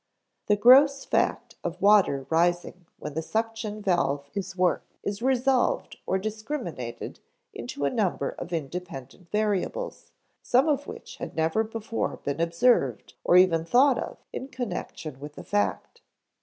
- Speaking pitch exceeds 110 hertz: Yes, high, 190 Hz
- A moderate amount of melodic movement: No, wide, 5.8 semitones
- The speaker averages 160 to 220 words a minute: No, average, 140 wpm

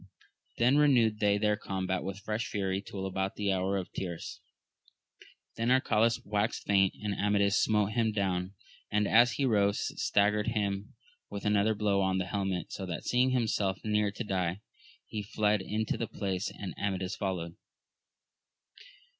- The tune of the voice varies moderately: No, narrow, 1.8 semitones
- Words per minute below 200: Yes, average, 155 wpm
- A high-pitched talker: No, low, 100 Hz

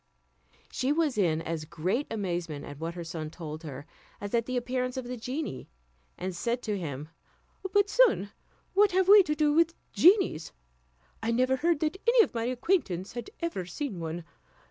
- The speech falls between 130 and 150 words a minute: No, average, 180 wpm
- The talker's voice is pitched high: Yes, high, 235 Hz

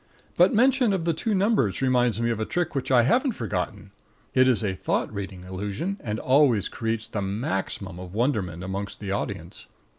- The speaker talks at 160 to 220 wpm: Yes, average, 185 wpm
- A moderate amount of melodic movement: No, wide, 6.6 semitones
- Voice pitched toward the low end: Yes, low, 115 Hz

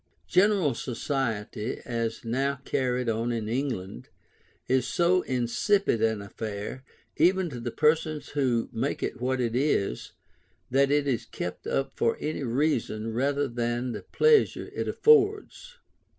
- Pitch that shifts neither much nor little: Yes, average, 4.4 semitones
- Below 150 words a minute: Yes, slow, 135 wpm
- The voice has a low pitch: Yes, low, 130 Hz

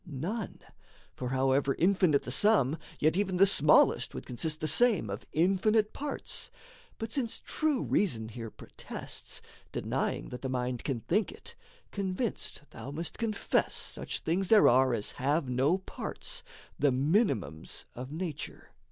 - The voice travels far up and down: Yes, wide, 7.4 semitones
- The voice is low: No, medium, 155 Hz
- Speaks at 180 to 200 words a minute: No, average, 145 wpm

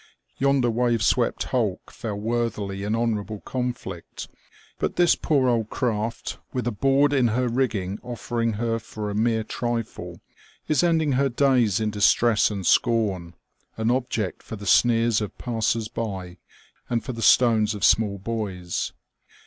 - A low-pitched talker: Yes, low, 115 Hz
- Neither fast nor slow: Yes, average, 150 wpm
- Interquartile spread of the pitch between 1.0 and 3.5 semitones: Yes, average, 2.8 semitones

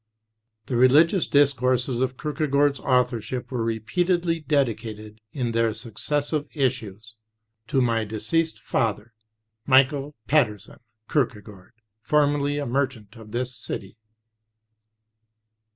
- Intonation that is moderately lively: Yes, average, 4.3 semitones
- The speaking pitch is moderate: No, low, 130 Hz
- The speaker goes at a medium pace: No, slow, 100 wpm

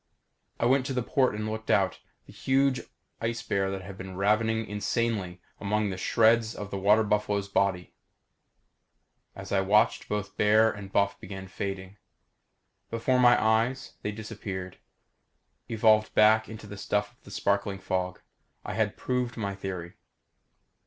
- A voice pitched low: Yes, low, 105 Hz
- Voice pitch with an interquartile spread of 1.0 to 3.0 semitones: Yes, narrow, 2.4 semitones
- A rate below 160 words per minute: Yes, average, 150 wpm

